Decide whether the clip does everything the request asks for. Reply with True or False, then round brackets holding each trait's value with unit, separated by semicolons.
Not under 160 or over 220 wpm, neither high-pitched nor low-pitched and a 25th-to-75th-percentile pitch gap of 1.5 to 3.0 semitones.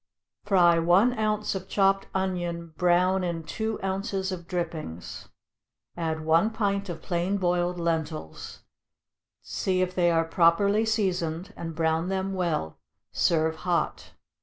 False (135 wpm; 180 Hz; 2.6 semitones)